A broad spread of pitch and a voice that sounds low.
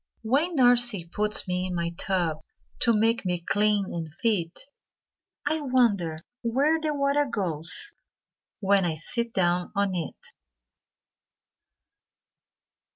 No: wide, 5.8 semitones; high, 205 Hz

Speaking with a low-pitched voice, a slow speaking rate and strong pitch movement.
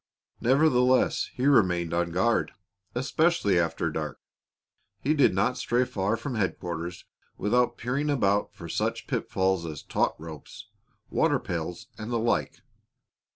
Yes: low, 105 Hz; slow, 130 wpm; wide, 6.5 semitones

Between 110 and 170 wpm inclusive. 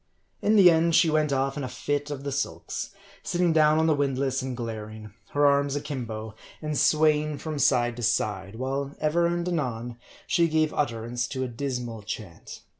No: average, 190 wpm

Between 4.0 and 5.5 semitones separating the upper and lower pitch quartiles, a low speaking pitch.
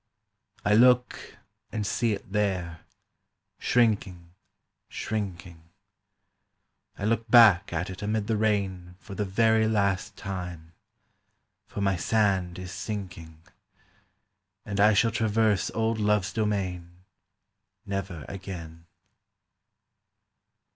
No: average, 3.2 semitones; low, 100 Hz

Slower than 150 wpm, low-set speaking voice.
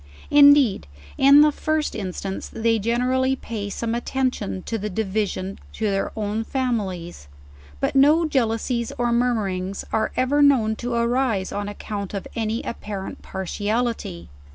No: average, 140 wpm; high, 225 Hz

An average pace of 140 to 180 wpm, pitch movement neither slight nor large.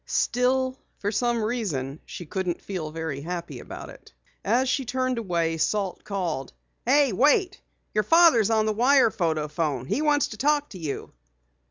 No: average, 165 wpm; wide, 7.6 semitones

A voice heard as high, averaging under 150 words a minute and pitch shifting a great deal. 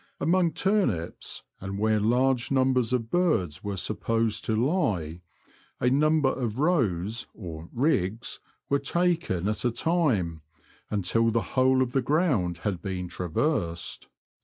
No: low, 115 Hz; average, 140 wpm; wide, 6.6 semitones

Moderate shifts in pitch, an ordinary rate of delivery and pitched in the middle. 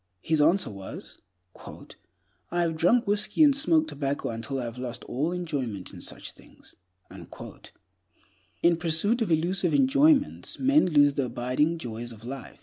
No: wide, 8.4 semitones; average, 145 wpm; medium, 160 Hz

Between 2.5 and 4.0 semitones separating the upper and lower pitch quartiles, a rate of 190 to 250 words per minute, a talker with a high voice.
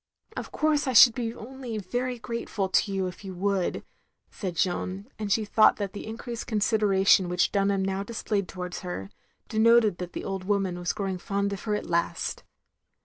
Yes: average, 2.9 semitones; average, 195 wpm; high, 200 Hz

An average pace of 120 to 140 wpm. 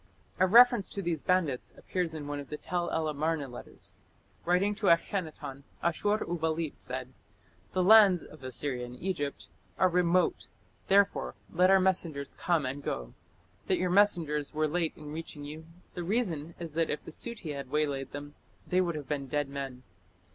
No: average, 175 wpm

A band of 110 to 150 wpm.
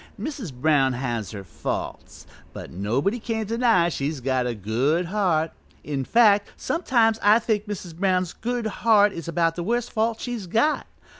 No: average, 165 wpm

